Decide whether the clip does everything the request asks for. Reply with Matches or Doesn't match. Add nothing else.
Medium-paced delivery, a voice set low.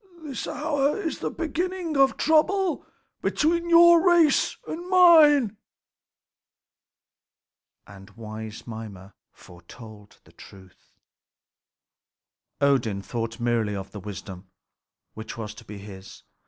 Doesn't match